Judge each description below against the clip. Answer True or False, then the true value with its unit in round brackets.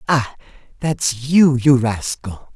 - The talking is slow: True (115 wpm)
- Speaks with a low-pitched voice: True (130 Hz)